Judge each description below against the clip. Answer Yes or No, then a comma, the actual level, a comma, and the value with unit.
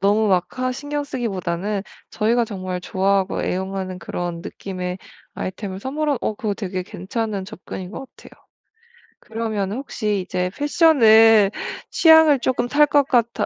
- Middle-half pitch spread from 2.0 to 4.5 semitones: No, average, 5.1 semitones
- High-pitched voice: Yes, high, 210 Hz